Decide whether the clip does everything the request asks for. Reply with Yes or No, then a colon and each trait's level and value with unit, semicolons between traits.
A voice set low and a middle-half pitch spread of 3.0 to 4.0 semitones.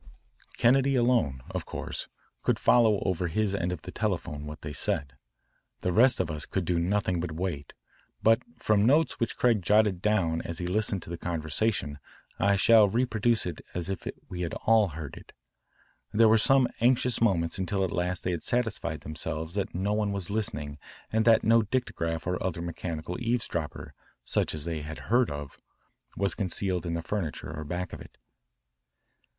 No: very low, 95 Hz; average, 4.9 semitones